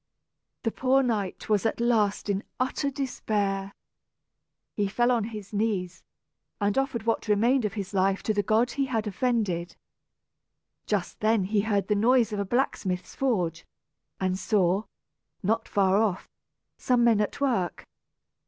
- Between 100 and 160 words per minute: Yes, average, 150 wpm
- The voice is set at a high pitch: Yes, high, 215 Hz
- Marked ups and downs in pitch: No, average, 3.3 semitones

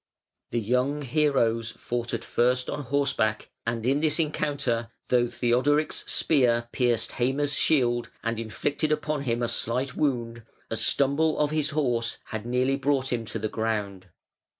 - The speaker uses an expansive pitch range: No, average, 3.7 semitones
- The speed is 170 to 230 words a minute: No, average, 150 wpm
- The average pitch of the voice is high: No, low, 125 Hz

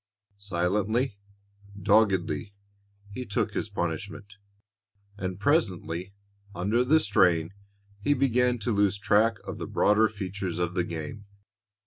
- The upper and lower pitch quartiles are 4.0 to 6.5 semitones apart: No, average, 3.3 semitones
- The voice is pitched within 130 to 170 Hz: No, low, 100 Hz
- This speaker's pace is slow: Yes, slow, 115 wpm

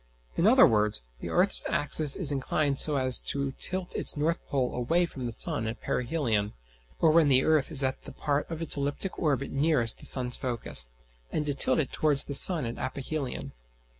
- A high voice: No, medium, 140 Hz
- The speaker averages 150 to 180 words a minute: No, average, 195 wpm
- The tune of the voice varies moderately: Yes, average, 3.6 semitones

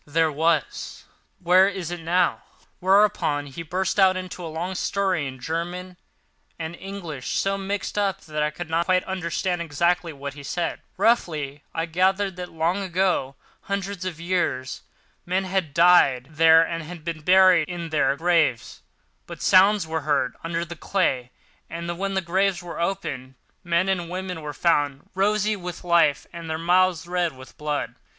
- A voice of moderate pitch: Yes, medium, 170 Hz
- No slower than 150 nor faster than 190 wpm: Yes, average, 165 wpm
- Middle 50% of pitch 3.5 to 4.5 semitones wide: No, average, 2.9 semitones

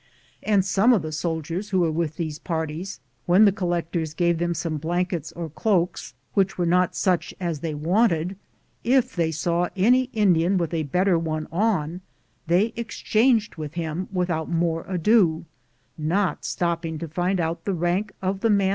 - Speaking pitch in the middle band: Yes, medium, 175 Hz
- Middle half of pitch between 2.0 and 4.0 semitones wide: Yes, average, 3.0 semitones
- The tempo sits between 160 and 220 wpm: Yes, average, 175 wpm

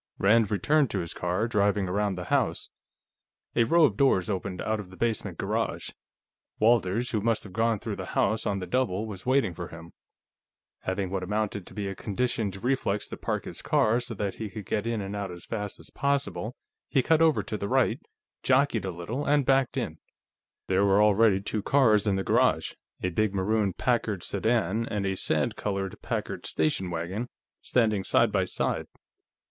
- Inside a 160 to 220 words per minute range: Yes, average, 185 wpm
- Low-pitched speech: Yes, low, 105 Hz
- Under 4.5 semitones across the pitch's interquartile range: Yes, average, 3.4 semitones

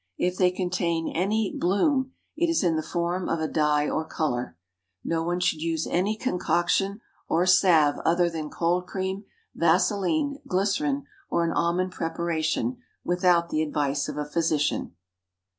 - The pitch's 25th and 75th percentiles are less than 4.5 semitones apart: Yes, average, 2.9 semitones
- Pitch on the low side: No, medium, 175 Hz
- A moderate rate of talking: Yes, average, 150 wpm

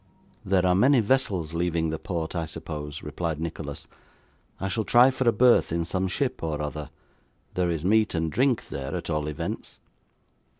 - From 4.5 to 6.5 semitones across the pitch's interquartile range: Yes, wide, 5.5 semitones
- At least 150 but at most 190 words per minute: Yes, average, 175 wpm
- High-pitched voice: No, very low, 85 Hz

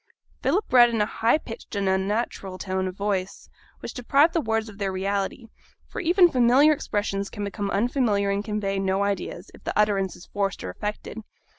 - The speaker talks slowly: No, average, 185 wpm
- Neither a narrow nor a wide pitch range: Yes, average, 3.2 semitones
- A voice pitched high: Yes, high, 205 Hz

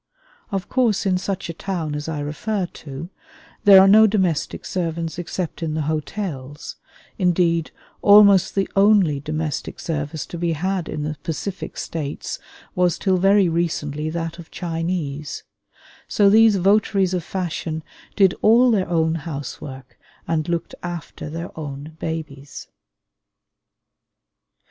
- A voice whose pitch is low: No, medium, 170 Hz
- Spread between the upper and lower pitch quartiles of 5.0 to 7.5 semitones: No, average, 3.7 semitones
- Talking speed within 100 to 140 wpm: Yes, slow, 135 wpm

